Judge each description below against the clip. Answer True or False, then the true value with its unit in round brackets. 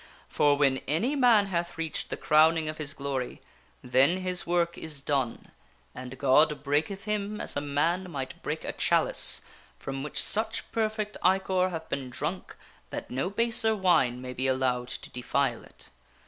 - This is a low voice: False (155 Hz)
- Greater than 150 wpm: True (165 wpm)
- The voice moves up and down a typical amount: False (5.8 semitones)